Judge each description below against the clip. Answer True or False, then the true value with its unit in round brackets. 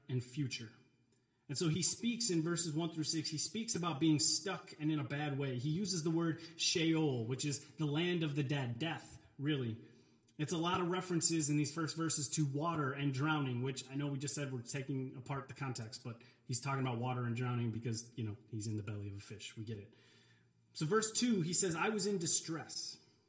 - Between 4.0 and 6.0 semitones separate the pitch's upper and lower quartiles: True (4.9 semitones)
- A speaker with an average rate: False (225 wpm)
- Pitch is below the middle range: False (145 Hz)